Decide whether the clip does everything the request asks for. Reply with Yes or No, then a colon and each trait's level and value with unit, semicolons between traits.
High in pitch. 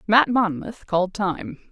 Yes: high, 200 Hz